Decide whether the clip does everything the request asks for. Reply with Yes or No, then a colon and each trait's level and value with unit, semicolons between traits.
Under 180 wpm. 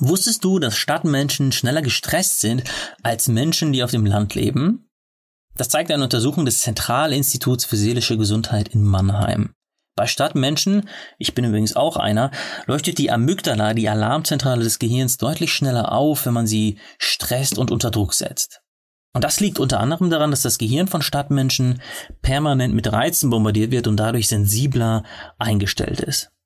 Yes: average, 160 wpm